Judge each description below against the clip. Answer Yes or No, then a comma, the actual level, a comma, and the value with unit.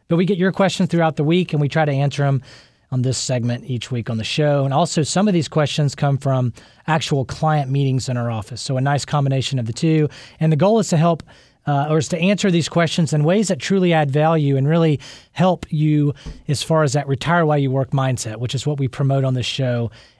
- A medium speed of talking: No, fast, 245 wpm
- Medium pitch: Yes, medium, 145 Hz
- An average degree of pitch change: Yes, average, 3.6 semitones